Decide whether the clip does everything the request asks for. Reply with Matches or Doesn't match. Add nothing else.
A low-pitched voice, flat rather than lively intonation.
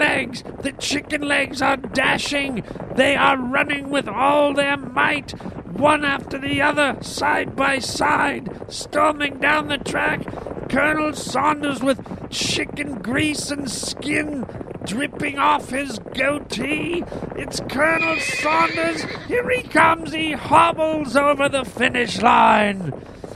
Doesn't match